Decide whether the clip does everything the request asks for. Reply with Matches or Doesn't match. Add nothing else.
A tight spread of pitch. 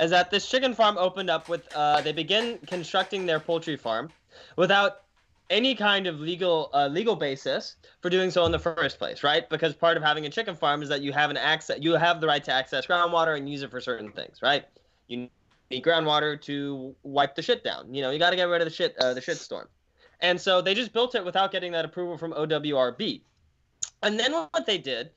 Doesn't match